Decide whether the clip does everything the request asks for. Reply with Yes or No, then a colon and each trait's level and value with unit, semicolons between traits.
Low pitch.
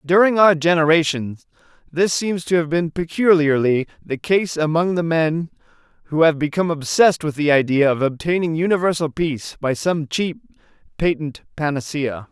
No: medium, 160 Hz